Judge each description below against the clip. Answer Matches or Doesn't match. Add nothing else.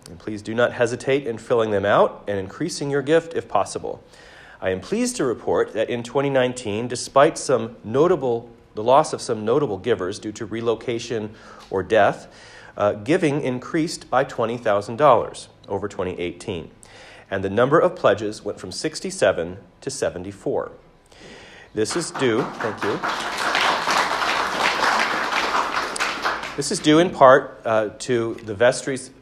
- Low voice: Matches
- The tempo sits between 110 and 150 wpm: Matches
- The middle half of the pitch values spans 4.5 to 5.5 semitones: Matches